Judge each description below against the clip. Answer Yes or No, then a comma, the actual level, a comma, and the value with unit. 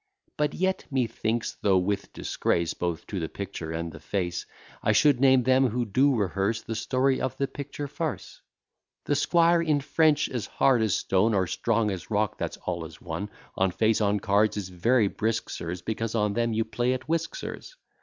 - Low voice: Yes, low, 110 Hz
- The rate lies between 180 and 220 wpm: Yes, average, 195 wpm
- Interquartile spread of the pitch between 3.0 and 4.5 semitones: No, wide, 5.4 semitones